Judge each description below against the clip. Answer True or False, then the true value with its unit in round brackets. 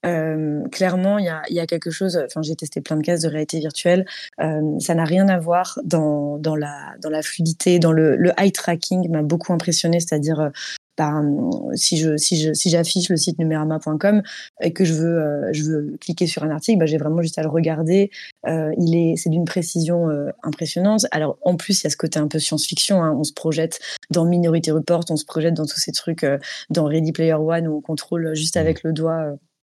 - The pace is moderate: False (230 wpm)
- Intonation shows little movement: True (1.9 semitones)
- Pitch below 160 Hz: False (165 Hz)